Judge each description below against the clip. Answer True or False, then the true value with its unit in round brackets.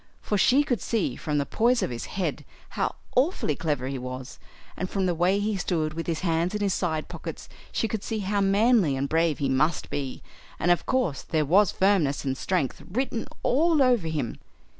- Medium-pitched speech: True (175 Hz)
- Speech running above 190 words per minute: True (205 wpm)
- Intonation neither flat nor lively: False (5.9 semitones)